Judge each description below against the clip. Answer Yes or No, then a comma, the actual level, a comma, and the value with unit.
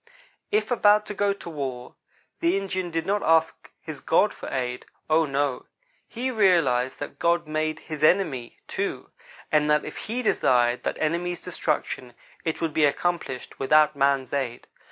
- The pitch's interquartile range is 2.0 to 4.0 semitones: No, average, 4.6 semitones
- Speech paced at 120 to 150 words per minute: No, average, 160 wpm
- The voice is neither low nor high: Yes, medium, 155 Hz